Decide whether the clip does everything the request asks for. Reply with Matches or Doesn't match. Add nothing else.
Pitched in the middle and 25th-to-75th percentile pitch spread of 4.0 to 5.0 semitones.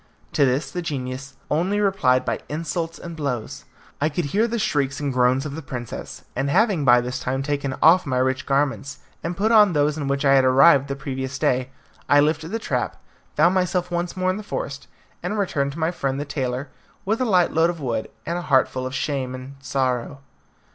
Matches